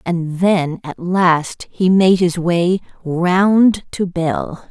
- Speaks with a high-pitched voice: No, medium, 175 Hz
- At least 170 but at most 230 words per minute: No, average, 140 wpm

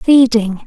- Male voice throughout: No, female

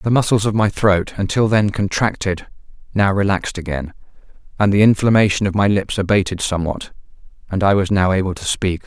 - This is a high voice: No, low, 100 Hz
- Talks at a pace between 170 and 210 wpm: Yes, average, 175 wpm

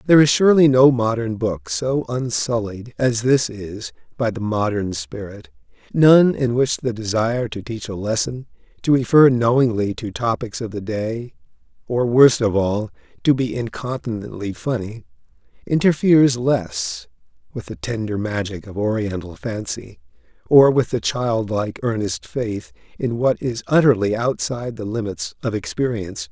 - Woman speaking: No, male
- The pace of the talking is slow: No, average, 145 wpm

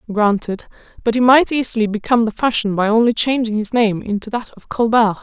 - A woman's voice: Yes, female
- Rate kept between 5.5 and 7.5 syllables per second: Yes, 5.9 syllables/s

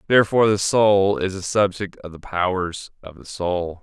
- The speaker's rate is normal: Yes, average, 190 wpm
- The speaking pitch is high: No, very low, 95 Hz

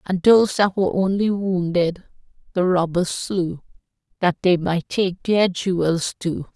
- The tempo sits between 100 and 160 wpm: Yes, average, 145 wpm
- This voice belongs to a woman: Yes, female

